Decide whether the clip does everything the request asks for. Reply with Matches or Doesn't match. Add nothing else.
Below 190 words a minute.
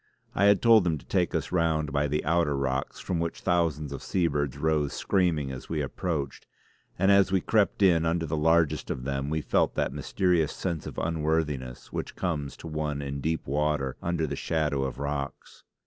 Doesn't match